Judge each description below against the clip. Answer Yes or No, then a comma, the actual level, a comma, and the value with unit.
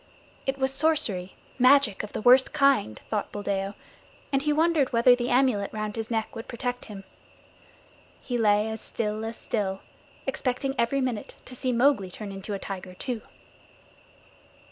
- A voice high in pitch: Yes, high, 230 Hz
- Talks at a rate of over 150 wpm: Yes, average, 160 wpm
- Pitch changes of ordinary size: Yes, average, 4.3 semitones